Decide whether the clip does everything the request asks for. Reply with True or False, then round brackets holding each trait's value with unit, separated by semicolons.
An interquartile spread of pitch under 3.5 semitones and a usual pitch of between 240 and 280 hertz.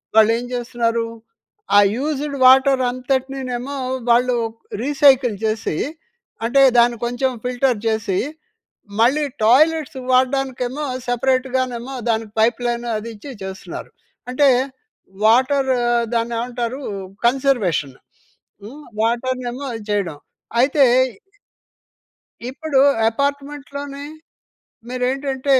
True (2.6 semitones; 255 Hz)